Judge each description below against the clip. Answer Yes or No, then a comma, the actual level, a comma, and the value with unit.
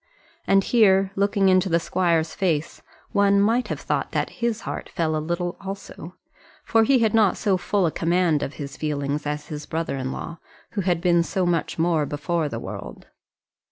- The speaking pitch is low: No, medium, 175 Hz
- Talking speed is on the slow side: No, average, 190 wpm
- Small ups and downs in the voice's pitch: No, average, 3.8 semitones